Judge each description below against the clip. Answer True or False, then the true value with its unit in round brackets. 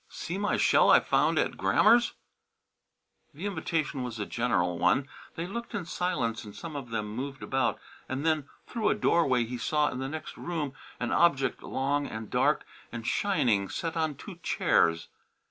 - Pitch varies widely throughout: True (6.1 semitones)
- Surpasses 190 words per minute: False (175 wpm)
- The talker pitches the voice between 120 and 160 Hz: True (140 Hz)